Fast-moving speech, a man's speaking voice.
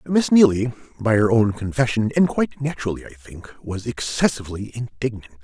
No: average, 155 wpm; male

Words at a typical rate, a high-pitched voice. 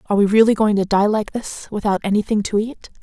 No: fast, 240 wpm; high, 210 Hz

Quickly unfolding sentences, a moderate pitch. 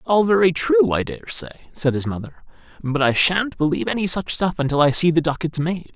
Yes: fast, 210 wpm; medium, 155 Hz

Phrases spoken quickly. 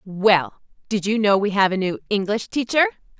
No: average, 170 wpm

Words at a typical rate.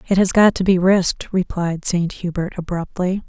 Yes: average, 185 wpm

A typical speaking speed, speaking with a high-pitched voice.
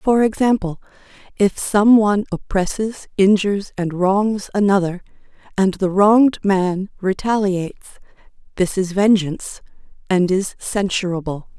No: slow, 105 wpm; high, 195 Hz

